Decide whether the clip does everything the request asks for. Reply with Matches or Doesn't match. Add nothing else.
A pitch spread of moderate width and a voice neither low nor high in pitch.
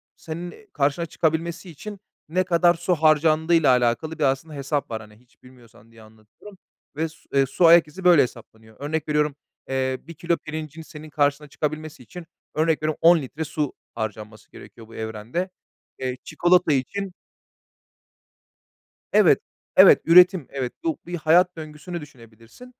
Matches